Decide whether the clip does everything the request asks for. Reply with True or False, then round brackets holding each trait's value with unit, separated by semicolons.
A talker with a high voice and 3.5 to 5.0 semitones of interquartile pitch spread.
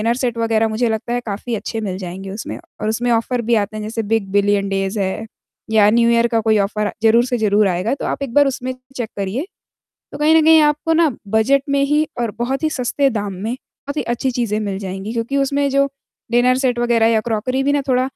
True (230 Hz; 3.8 semitones)